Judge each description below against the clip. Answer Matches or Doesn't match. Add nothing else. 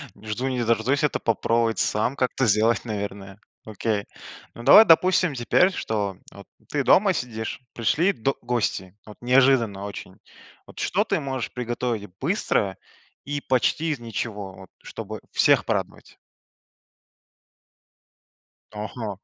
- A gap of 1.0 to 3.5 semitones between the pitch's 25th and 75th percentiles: Doesn't match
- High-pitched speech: Doesn't match